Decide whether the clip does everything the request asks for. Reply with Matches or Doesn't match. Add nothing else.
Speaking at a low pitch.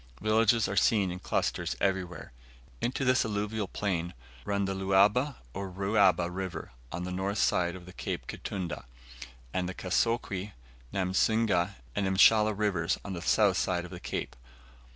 Matches